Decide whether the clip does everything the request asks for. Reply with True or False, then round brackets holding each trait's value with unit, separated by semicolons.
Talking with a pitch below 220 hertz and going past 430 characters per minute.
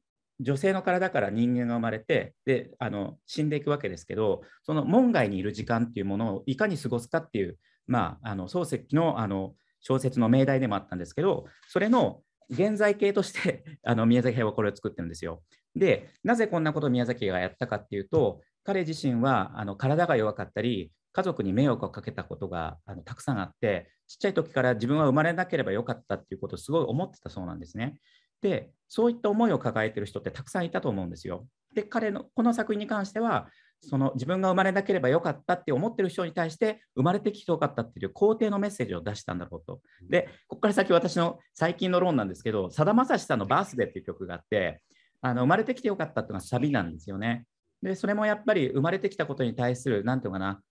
True (135 Hz; 470 characters per minute)